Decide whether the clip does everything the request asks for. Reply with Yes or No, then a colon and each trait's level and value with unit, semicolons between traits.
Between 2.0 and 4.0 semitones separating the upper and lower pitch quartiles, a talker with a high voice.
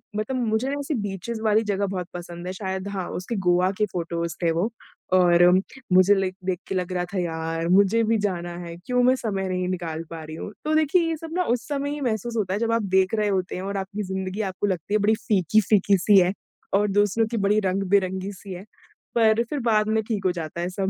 Yes: average, 3.3 semitones; high, 195 Hz